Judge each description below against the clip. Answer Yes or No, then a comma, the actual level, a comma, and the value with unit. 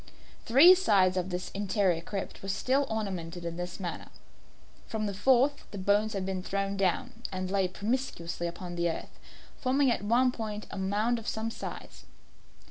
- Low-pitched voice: No, high, 200 Hz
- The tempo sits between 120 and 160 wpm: No, average, 175 wpm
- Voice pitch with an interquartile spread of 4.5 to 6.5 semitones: No, average, 3.8 semitones